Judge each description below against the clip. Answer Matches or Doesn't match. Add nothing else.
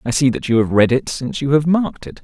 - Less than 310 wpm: Doesn't match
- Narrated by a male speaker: Matches